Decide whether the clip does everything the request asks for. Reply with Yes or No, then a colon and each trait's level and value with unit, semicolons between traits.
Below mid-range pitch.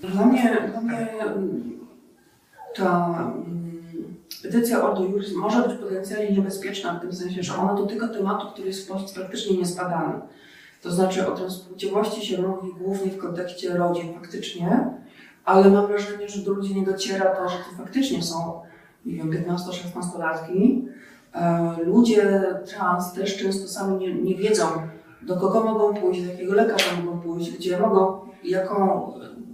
No: high, 190 Hz